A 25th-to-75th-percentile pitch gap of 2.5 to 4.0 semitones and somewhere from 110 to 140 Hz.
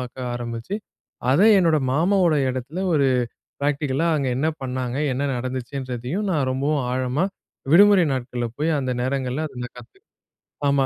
Yes: average, 3.4 semitones; low, 135 Hz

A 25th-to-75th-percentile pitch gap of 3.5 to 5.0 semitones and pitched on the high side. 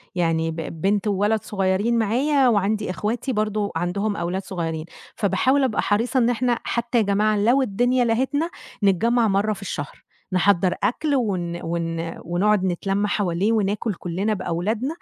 Yes: average, 4.1 semitones; high, 205 Hz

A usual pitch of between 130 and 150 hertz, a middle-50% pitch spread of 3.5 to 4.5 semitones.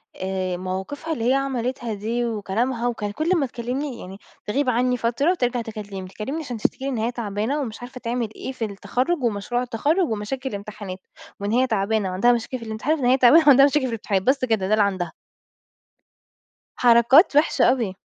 No: high, 235 Hz; average, 3.9 semitones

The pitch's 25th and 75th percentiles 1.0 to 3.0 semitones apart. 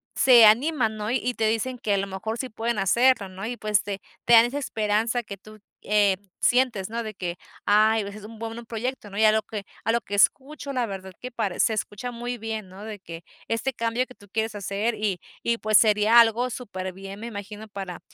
Yes: average, 2.7 semitones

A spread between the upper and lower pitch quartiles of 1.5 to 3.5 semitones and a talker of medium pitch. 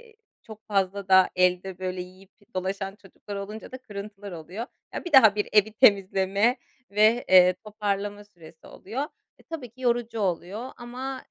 No: average, 3.2 semitones; high, 205 Hz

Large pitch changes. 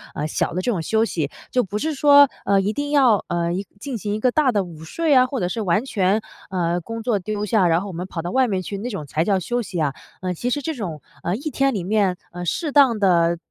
Yes: wide, 6.0 semitones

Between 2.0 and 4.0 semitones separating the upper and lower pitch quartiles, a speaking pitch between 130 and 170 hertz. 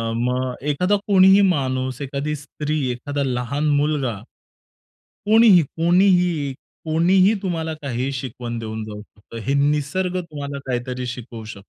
No: average, 5.0 semitones; medium, 140 Hz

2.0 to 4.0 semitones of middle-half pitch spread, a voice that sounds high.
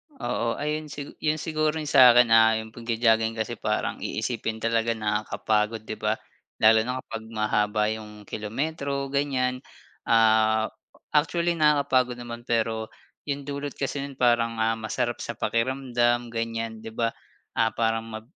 No: average, 3.4 semitones; low, 115 Hz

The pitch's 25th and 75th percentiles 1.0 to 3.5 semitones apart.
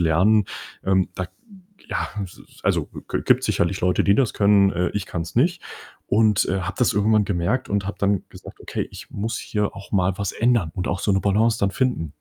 Yes: average, 2.7 semitones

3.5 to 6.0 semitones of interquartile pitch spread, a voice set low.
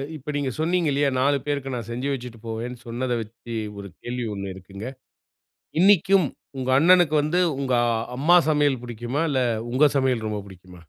Yes: average, 4.2 semitones; low, 130 Hz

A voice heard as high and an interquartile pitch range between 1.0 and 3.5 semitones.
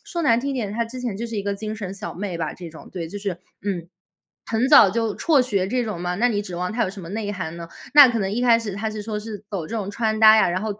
Yes: high, 210 Hz; average, 3.2 semitones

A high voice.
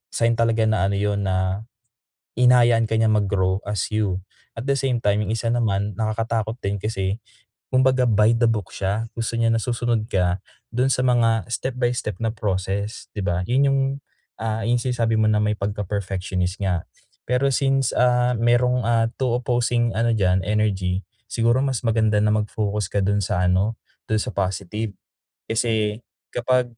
No: low, 110 Hz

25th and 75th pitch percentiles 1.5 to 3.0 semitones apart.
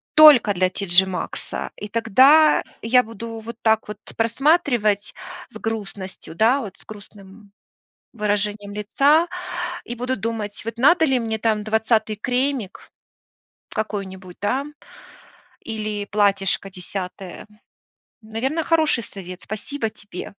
No: average, 3.4 semitones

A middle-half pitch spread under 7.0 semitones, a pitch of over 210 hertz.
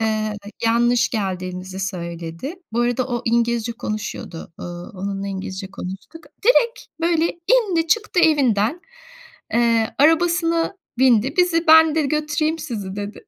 No: wide, 8.3 semitones; high, 235 Hz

